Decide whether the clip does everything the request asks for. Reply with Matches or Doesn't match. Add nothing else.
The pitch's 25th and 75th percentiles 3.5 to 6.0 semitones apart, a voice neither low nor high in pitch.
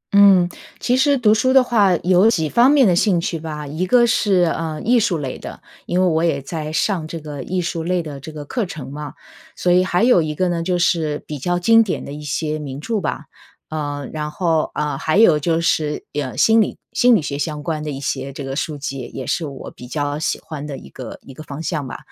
Matches